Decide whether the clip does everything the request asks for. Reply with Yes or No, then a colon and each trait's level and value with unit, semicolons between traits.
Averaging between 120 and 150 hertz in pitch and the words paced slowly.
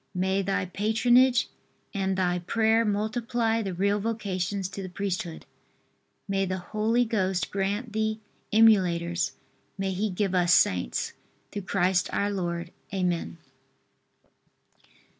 No: high, 195 Hz; slow, 120 wpm